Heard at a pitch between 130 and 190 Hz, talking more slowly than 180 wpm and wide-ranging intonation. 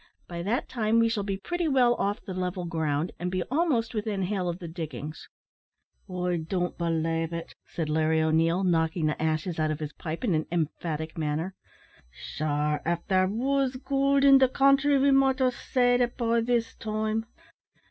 No: medium, 185 Hz; average, 185 wpm; wide, 6.9 semitones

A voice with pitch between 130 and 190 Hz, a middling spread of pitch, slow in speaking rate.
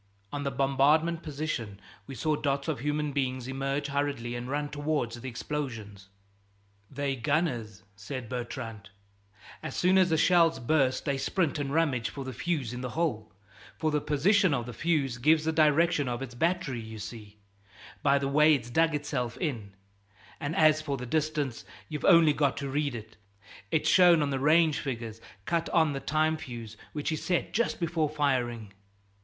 No: medium, 140 Hz; average, 4.2 semitones; average, 175 wpm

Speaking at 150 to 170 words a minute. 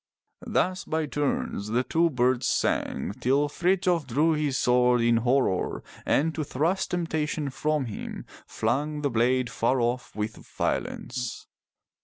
No: average, 140 wpm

